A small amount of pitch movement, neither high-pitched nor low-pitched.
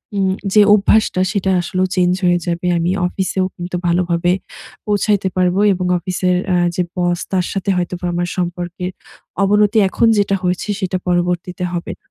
Yes: narrow, 1.5 semitones; medium, 180 Hz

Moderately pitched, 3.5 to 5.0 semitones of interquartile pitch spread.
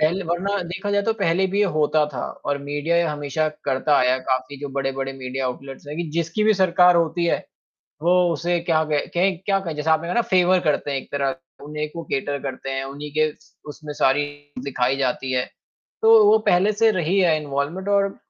Yes: medium, 155 Hz; average, 4.4 semitones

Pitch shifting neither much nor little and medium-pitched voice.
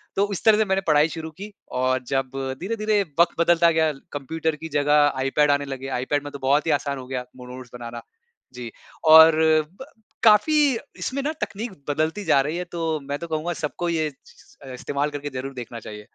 Yes: average, 3.9 semitones; medium, 150 Hz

